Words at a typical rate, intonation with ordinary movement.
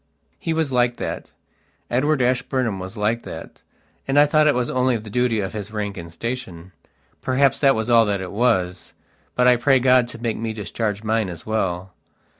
Yes: average, 190 wpm; average, 3.7 semitones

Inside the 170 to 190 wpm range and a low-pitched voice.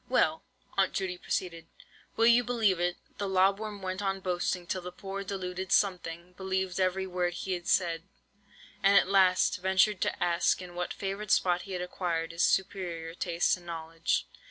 No: average, 175 wpm; medium, 185 Hz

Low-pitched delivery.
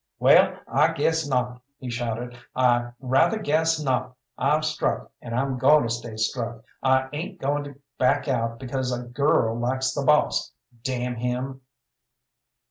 Yes: low, 130 Hz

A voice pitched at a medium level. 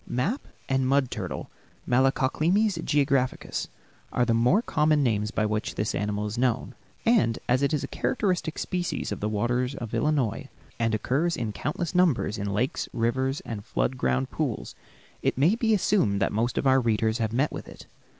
No: low, 130 Hz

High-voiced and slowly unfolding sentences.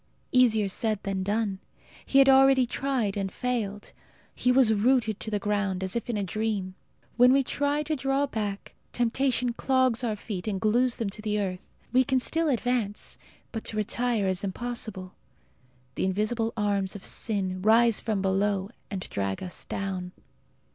No: high, 215 Hz; average, 170 wpm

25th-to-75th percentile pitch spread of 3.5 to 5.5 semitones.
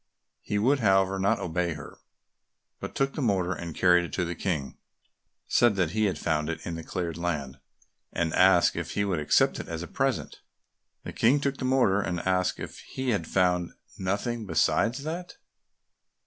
Yes: average, 4.8 semitones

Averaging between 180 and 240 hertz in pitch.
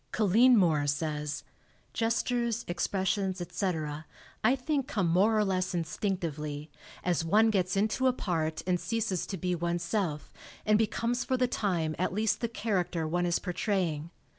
Yes: medium, 185 Hz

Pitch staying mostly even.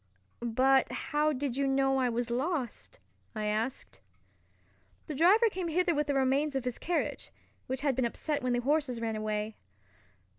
No: average, 3.8 semitones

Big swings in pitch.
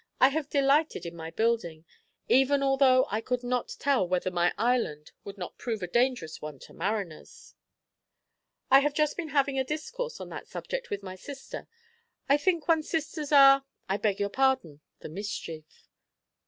Yes: wide, 7.2 semitones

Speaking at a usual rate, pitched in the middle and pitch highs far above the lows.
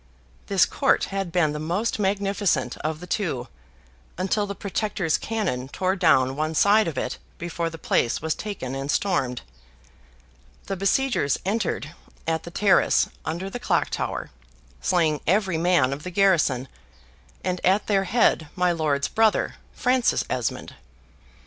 No: average, 145 wpm; medium, 180 Hz; average, 4.7 semitones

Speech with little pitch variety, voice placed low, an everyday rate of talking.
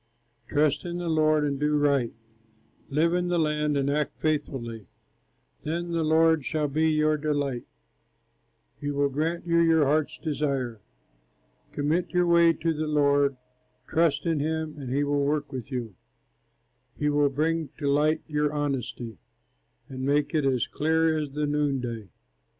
No: narrow, 2.1 semitones; medium, 150 Hz; average, 155 wpm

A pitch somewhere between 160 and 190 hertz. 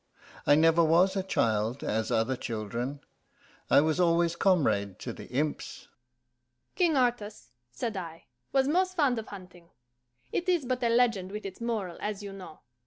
Yes: medium, 185 Hz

